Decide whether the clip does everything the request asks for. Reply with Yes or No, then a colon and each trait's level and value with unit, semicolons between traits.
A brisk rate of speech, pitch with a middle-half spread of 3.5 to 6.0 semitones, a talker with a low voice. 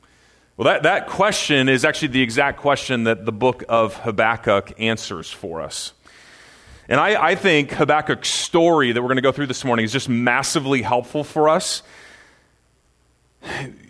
No: average, 160 wpm; average, 4.0 semitones; low, 130 Hz